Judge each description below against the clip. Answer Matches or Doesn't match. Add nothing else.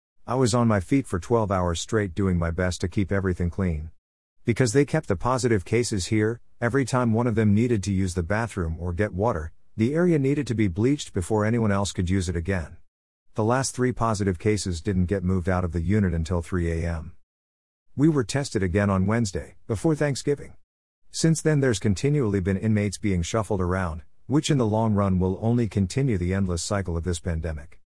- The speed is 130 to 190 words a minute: Doesn't match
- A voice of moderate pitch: Doesn't match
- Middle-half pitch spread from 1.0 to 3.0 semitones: Doesn't match